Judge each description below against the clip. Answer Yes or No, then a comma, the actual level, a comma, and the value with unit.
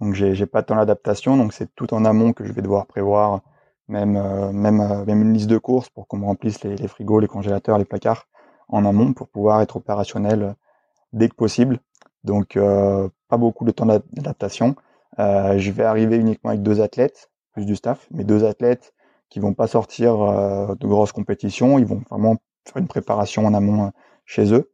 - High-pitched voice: No, low, 105 Hz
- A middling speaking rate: Yes, average, 205 wpm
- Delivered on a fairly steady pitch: Yes, narrow, 2.0 semitones